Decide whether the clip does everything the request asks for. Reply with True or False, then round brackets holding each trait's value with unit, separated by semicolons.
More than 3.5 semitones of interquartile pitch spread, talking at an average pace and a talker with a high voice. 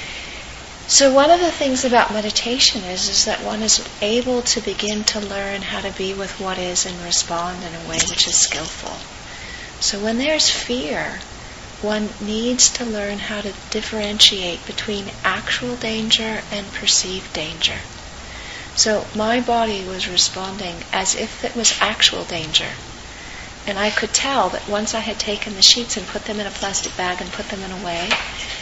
False (2.8 semitones; 175 wpm; 210 Hz)